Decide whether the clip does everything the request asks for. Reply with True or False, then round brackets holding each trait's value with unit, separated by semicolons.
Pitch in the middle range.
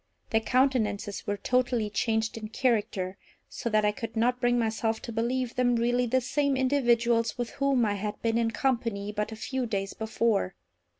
False (230 Hz)